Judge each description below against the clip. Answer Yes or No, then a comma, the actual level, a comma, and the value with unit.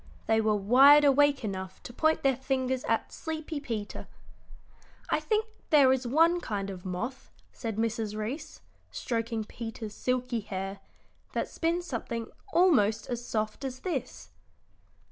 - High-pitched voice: Yes, high, 245 Hz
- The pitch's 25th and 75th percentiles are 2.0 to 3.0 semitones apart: No, average, 4.7 semitones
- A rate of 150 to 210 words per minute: No, average, 140 wpm